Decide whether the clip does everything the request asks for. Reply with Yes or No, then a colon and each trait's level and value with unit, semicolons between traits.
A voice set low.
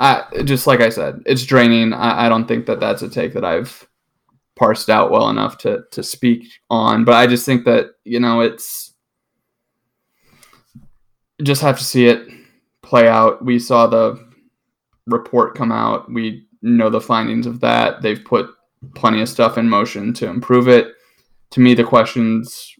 Yes: low, 120 Hz